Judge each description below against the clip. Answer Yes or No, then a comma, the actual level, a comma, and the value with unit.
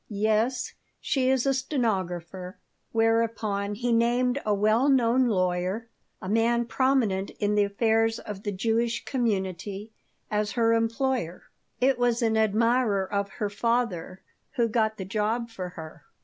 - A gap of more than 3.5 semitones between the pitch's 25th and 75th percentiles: No, average, 2.9 semitones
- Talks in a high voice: Yes, high, 225 Hz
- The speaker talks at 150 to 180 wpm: No, average, 140 wpm